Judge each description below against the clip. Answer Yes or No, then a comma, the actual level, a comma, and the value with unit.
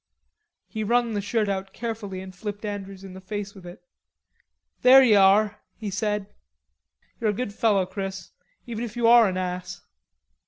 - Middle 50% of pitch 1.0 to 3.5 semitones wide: Yes, narrow, 2.5 semitones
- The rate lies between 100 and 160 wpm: No, average, 170 wpm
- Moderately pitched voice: No, high, 205 Hz